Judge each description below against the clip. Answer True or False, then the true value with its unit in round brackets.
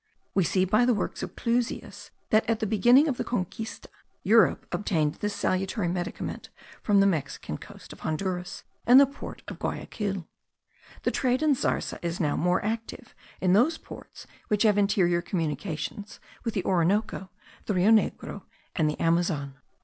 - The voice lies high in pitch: True (195 Hz)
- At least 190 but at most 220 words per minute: False (165 wpm)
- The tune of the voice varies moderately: True (4.2 semitones)